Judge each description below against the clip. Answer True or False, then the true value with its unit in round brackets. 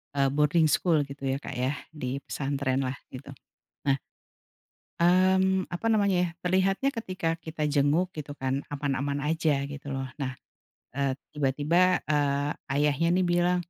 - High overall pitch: False (150 Hz)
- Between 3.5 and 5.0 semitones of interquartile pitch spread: True (4.1 semitones)